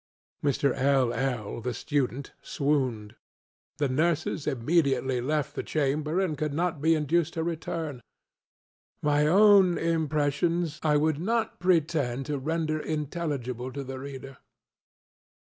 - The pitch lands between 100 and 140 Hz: No, medium, 150 Hz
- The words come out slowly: Yes, slow, 120 wpm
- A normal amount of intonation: Yes, average, 3.3 semitones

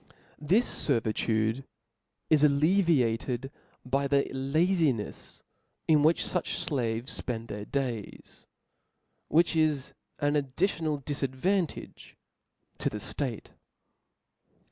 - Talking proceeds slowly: Yes, slow, 95 wpm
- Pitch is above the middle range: No, medium, 140 Hz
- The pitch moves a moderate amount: Yes, average, 4.3 semitones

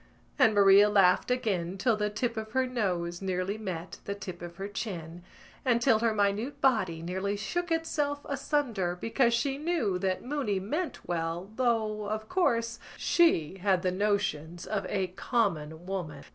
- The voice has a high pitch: Yes, high, 205 Hz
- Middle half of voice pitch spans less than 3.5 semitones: No, average, 4.6 semitones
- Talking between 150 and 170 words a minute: Yes, average, 160 wpm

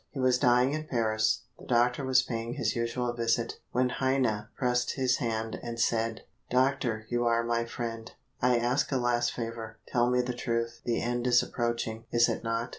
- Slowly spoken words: No, average, 190 wpm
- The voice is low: Yes, low, 120 Hz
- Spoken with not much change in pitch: Yes, narrow, 1.3 semitones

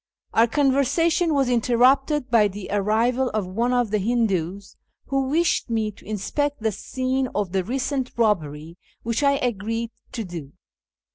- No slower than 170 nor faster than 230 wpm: No, average, 155 wpm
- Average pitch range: Yes, average, 4.3 semitones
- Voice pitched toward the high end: Yes, high, 230 Hz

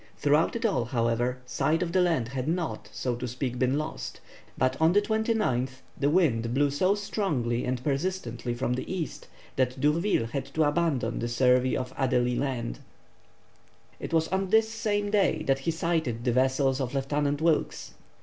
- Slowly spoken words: No, average, 175 wpm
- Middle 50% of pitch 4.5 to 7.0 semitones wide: Yes, average, 5.1 semitones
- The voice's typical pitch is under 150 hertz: Yes, medium, 140 Hz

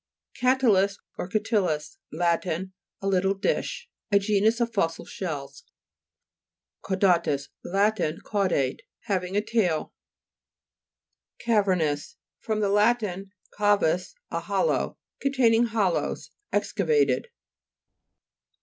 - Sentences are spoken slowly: Yes, slow, 105 wpm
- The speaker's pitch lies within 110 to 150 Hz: No, high, 195 Hz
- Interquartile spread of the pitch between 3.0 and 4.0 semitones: Yes, average, 3.7 semitones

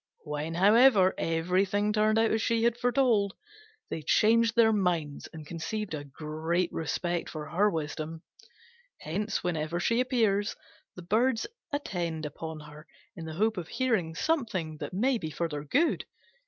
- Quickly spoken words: No, average, 155 wpm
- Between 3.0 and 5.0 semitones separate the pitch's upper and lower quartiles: No, wide, 5.6 semitones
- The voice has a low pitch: No, medium, 185 Hz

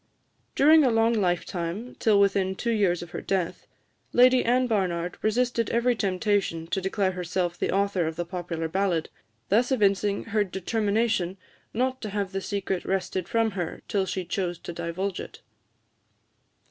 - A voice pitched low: No, high, 195 Hz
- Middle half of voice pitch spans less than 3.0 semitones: No, average, 3.9 semitones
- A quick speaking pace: No, average, 160 wpm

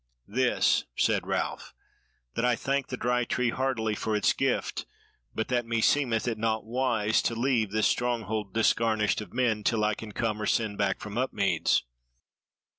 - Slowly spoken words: No, average, 165 wpm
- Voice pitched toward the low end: Yes, low, 115 Hz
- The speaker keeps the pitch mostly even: Yes, narrow, 2.3 semitones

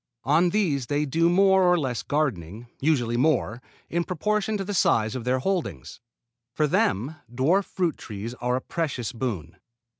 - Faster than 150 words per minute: Yes, average, 160 wpm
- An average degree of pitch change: No, wide, 6.5 semitones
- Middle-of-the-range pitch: Yes, medium, 145 Hz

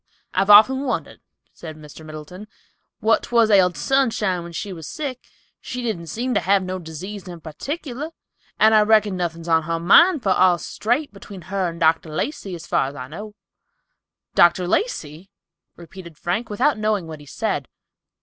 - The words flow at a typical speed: Yes, average, 170 wpm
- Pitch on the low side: No, medium, 185 Hz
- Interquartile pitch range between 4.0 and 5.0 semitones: Yes, average, 4.7 semitones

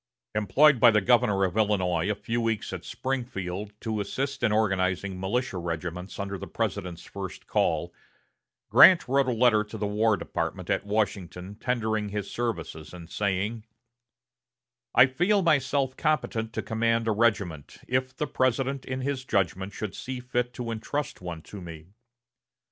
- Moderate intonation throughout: Yes, average, 4.7 semitones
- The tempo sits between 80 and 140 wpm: No, average, 155 wpm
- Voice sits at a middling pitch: No, low, 110 Hz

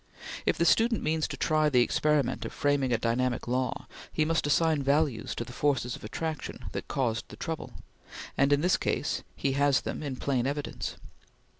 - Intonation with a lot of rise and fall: No, average, 3.3 semitones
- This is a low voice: No, medium, 145 Hz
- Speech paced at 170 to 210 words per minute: Yes, average, 185 wpm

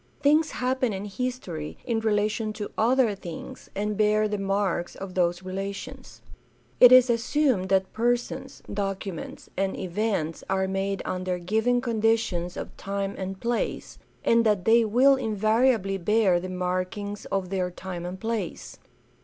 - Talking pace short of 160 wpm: Yes, average, 145 wpm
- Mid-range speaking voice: No, high, 205 Hz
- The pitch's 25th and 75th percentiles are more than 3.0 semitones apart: Yes, average, 3.5 semitones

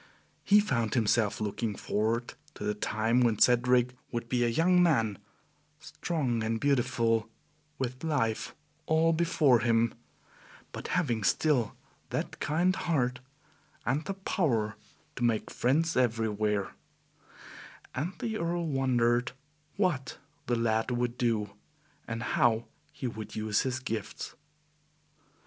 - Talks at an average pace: No, slow, 125 wpm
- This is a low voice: Yes, low, 120 Hz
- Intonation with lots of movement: No, average, 4.6 semitones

